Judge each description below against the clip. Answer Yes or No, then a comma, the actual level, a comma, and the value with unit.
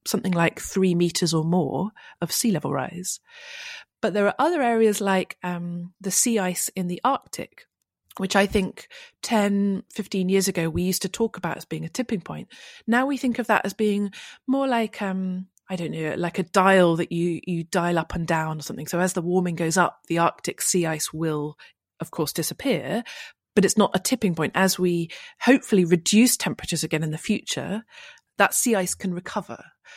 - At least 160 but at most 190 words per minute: No, average, 200 wpm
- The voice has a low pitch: No, medium, 185 Hz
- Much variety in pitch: No, average, 3.7 semitones